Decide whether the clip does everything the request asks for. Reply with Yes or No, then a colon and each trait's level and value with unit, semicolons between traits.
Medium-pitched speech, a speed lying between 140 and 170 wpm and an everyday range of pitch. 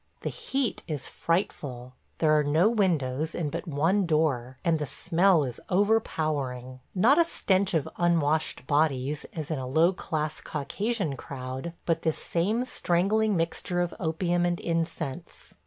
Yes: medium, 165 Hz; average, 150 wpm; average, 3.9 semitones